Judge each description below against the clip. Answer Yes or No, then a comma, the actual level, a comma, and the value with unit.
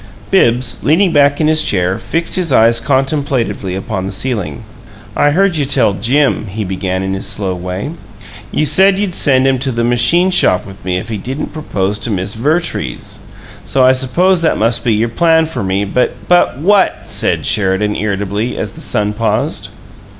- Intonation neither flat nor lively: No, wide, 7.2 semitones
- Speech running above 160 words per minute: Yes, average, 185 wpm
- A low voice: Yes, low, 120 Hz